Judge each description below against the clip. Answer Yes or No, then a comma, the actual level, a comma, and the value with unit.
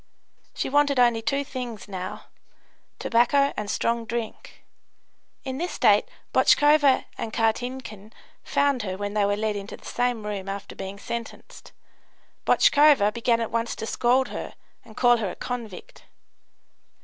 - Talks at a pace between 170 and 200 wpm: No, average, 145 wpm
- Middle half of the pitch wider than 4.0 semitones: No, average, 3.6 semitones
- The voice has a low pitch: No, high, 230 Hz